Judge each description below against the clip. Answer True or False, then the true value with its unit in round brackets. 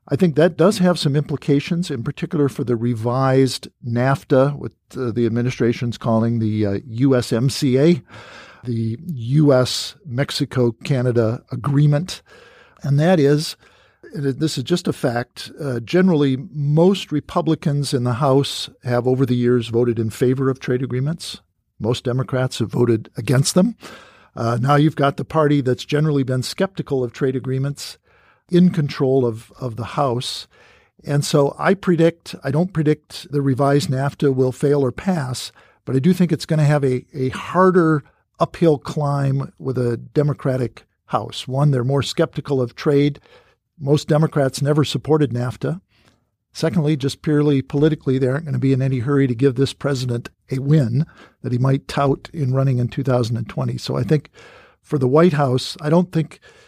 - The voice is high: False (140 Hz)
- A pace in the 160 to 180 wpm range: True (165 wpm)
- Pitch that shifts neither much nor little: True (3.3 semitones)